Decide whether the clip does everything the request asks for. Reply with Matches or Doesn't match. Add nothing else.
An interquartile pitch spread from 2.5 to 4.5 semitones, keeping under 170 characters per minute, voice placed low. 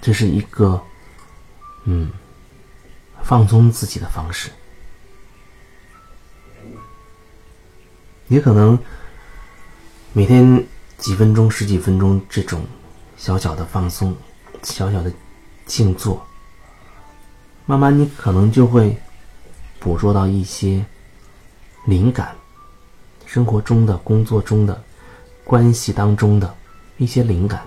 Matches